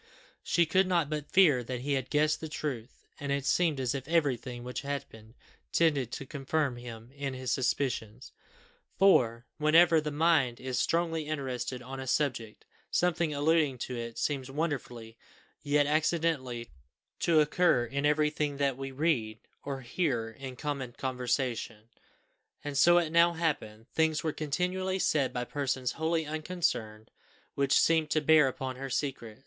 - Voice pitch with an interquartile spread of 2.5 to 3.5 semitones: No, average, 3.9 semitones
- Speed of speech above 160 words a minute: No, average, 155 wpm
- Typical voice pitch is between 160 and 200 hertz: No, medium, 140 Hz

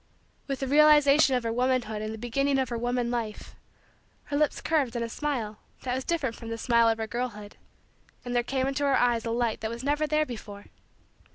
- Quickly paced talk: Yes, fast, 210 wpm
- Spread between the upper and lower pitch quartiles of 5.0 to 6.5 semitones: No, average, 3.2 semitones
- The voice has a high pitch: Yes, high, 245 Hz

